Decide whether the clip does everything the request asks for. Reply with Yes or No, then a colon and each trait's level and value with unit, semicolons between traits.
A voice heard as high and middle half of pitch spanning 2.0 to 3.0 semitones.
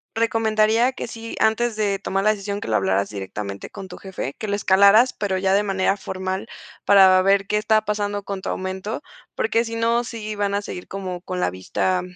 Yes: high, 200 Hz; narrow, 2.5 semitones